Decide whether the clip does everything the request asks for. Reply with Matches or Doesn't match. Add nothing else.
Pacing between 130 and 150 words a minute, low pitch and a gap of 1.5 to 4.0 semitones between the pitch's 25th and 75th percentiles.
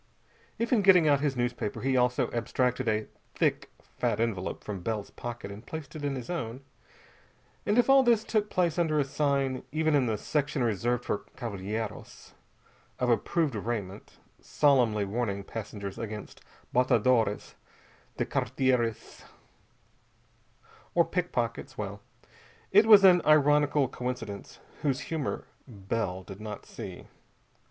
Doesn't match